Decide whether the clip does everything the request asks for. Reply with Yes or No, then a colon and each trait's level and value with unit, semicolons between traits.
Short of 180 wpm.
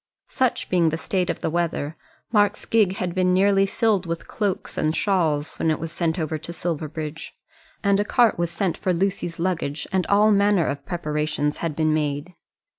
No: average, 190 wpm